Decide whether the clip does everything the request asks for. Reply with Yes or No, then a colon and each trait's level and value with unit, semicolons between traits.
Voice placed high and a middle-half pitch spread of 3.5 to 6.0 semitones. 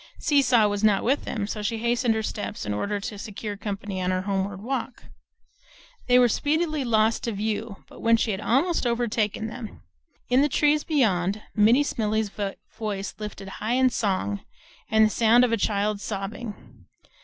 No: high, 220 Hz; average, 3.1 semitones